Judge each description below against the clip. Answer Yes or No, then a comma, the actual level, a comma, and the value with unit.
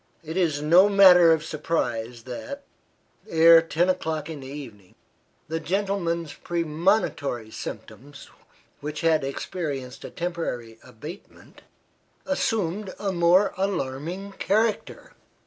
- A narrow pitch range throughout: No, average, 4.6 semitones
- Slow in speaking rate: Yes, slow, 110 wpm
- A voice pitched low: No, medium, 165 Hz